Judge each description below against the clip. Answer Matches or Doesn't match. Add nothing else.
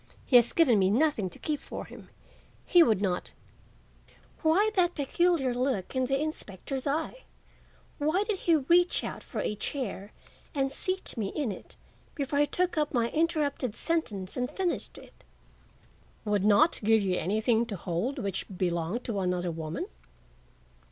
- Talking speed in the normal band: Matches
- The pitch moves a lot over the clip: Matches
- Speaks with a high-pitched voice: Matches